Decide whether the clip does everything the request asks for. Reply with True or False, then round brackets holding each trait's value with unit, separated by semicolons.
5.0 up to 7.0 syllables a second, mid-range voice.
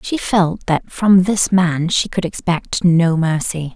False (3.6 syllables/s; 175 Hz)